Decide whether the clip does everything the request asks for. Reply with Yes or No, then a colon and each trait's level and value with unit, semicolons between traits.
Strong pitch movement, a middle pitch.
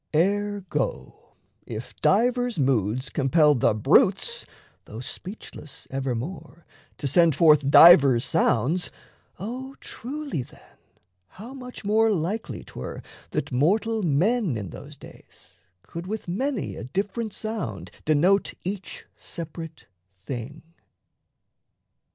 Yes: wide, 8.0 semitones; medium, 170 Hz